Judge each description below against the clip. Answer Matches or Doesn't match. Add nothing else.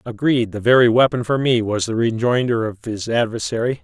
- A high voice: Doesn't match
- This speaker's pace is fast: Doesn't match